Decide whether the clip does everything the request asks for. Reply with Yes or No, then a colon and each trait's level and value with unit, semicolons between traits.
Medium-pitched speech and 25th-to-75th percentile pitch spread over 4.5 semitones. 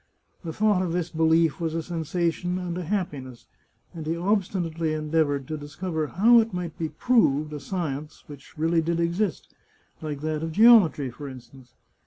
No: medium, 165 Hz; average, 2.9 semitones